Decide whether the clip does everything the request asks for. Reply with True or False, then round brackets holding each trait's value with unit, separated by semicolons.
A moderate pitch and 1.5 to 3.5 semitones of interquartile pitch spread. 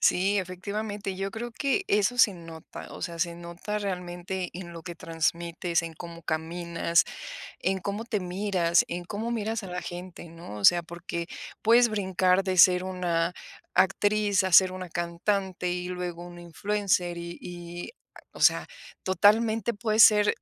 True (180 Hz; 3.0 semitones)